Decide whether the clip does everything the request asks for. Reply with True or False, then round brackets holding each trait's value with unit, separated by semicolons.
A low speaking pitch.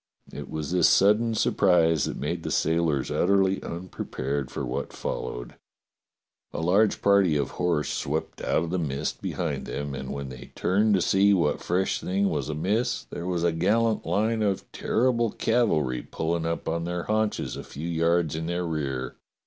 True (85 Hz)